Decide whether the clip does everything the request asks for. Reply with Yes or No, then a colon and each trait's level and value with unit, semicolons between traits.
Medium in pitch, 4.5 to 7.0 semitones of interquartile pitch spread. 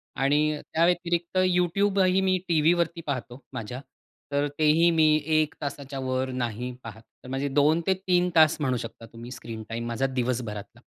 Yes: medium, 145 Hz; average, 5.2 semitones